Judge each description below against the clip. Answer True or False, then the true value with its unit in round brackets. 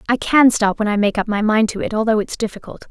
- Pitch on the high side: True (220 Hz)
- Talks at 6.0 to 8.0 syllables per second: True (6.3 syllables/s)